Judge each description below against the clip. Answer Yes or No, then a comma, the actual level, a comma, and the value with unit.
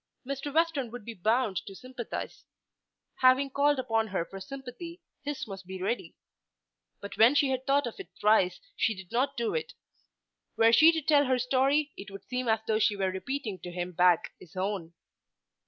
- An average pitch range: No, wide, 5.8 semitones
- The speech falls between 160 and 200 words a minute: Yes, average, 190 wpm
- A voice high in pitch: Yes, high, 235 Hz